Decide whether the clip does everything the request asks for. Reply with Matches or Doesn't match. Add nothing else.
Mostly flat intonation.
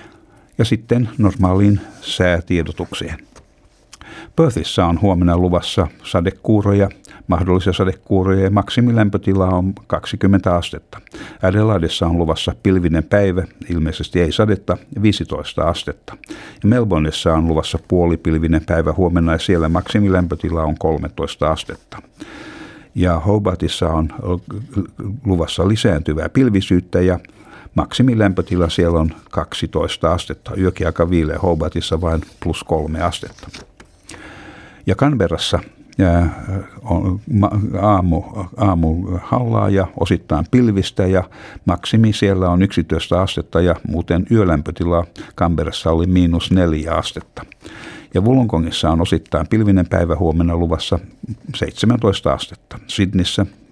Doesn't match